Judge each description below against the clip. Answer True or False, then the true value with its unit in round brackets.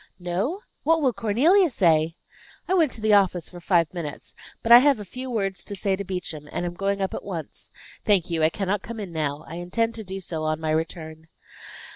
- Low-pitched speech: False (190 Hz)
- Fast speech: True (220 wpm)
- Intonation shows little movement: False (5.0 semitones)